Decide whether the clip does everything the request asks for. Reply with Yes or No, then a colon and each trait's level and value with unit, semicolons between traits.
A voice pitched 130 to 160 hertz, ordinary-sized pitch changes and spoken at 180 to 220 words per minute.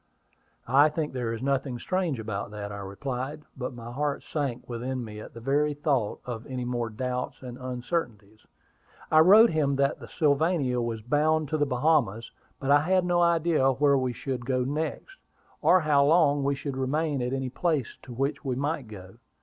Yes: low, 135 Hz; average, 3.6 semitones; average, 190 wpm